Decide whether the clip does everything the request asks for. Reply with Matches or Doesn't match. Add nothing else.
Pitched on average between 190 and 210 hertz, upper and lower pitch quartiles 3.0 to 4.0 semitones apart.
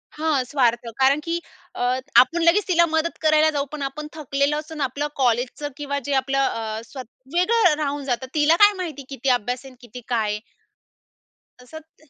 Doesn't match